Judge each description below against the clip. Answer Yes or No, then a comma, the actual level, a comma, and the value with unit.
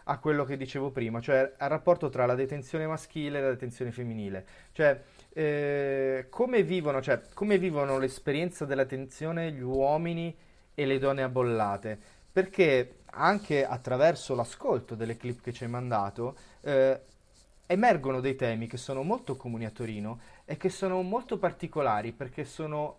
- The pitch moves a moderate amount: Yes, average, 3.9 semitones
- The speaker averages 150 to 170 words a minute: Yes, average, 155 wpm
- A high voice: No, low, 135 Hz